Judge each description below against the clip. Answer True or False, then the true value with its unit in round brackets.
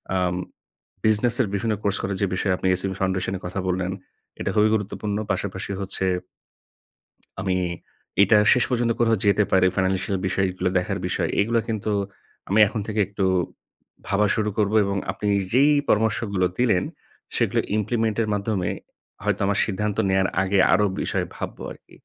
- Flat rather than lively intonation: True (2.3 semitones)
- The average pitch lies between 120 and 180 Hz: False (100 Hz)